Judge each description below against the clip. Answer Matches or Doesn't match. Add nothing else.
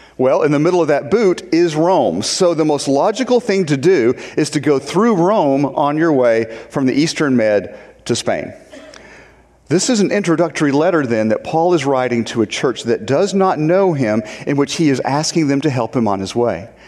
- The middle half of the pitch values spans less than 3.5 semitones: Doesn't match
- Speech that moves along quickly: Matches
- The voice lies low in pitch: Doesn't match